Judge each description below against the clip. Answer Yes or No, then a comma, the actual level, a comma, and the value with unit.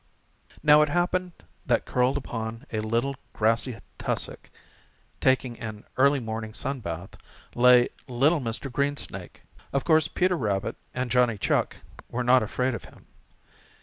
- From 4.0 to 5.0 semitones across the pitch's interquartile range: No, average, 3.6 semitones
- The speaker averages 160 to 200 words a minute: No, average, 145 wpm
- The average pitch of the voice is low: Yes, low, 125 Hz